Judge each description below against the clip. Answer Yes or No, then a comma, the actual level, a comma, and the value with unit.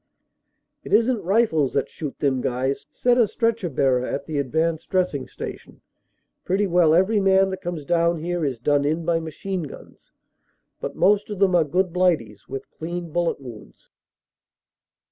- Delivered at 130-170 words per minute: Yes, average, 165 wpm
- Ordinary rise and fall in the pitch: Yes, average, 4.9 semitones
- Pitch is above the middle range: No, medium, 170 Hz